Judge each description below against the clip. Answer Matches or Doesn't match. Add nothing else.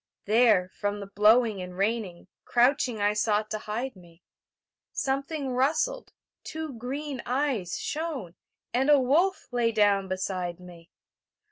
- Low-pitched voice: Doesn't match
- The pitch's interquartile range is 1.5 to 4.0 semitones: Doesn't match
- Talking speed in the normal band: Doesn't match